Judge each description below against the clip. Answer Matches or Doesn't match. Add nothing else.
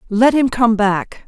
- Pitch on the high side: Matches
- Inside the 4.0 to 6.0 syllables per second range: Doesn't match